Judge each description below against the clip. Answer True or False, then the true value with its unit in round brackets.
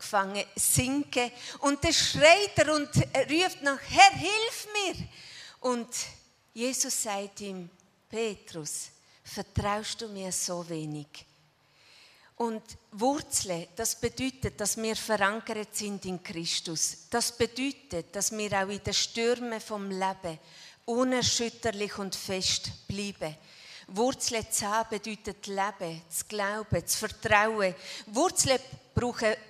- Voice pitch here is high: True (215 Hz)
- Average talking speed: False (115 wpm)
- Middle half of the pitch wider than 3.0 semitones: True (4.2 semitones)